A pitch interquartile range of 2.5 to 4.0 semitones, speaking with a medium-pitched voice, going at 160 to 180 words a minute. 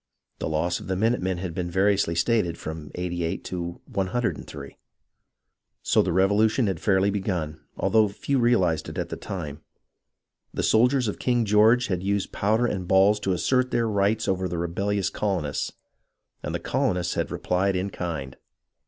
No: average, 3.5 semitones; very low, 95 Hz; average, 170 wpm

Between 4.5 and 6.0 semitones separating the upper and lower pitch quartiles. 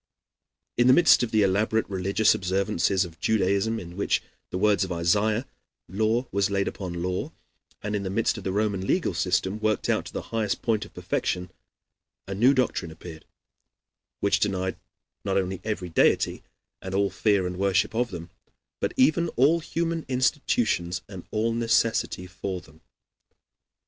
No: average, 3.3 semitones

